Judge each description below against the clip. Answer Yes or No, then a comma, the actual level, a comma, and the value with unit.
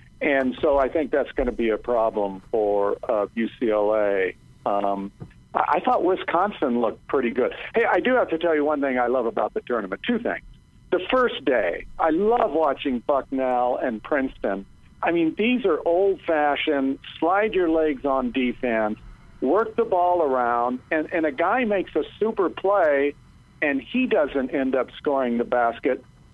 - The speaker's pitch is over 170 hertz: No, medium, 140 Hz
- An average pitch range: No, wide, 6.3 semitones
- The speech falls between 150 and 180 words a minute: Yes, average, 175 wpm